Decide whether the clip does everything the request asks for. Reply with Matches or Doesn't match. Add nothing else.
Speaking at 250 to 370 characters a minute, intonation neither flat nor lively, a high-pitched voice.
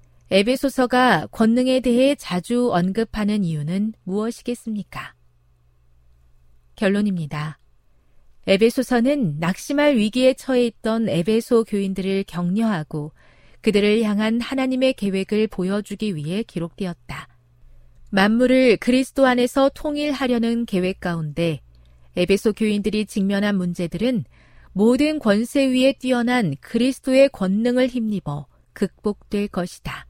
Doesn't match